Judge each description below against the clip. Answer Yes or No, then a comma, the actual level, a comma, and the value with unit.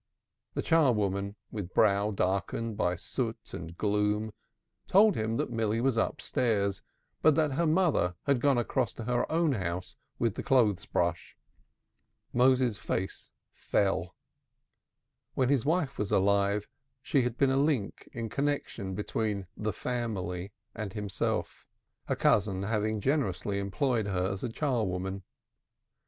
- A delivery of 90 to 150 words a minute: Yes, average, 140 wpm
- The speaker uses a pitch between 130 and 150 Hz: No, low, 110 Hz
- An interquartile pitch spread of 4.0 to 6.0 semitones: Yes, average, 4.6 semitones